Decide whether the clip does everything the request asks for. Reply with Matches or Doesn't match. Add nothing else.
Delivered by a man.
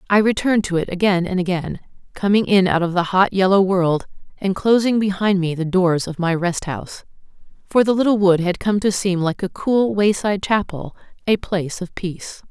Doesn't match